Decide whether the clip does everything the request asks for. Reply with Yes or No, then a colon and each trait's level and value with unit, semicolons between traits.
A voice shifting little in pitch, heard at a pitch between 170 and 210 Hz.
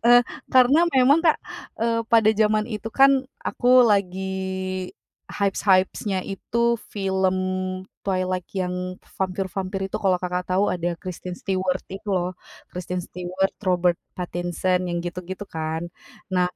Yes: narrow, 2.2 semitones; medium, 185 Hz